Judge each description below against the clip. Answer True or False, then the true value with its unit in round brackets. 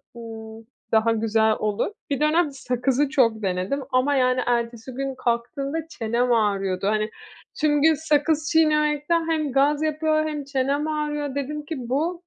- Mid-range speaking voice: False (275 Hz)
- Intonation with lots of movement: False (4.5 semitones)